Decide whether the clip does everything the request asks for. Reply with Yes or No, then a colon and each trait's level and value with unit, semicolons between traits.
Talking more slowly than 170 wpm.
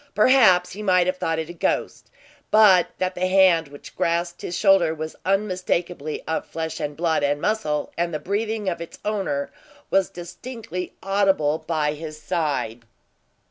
Yes: average, 160 wpm